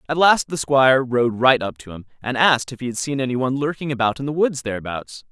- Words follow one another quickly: Yes, fast, 260 wpm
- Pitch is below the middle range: Yes, low, 130 Hz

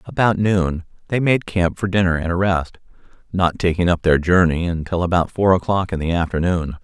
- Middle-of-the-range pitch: No, very low, 90 Hz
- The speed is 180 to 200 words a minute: Yes, average, 195 wpm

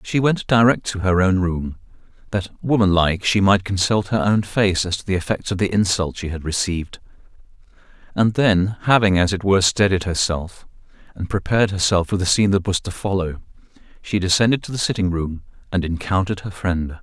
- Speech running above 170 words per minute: Yes, average, 190 wpm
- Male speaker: Yes, male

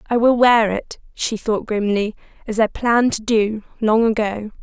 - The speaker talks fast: No, average, 180 wpm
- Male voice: No, female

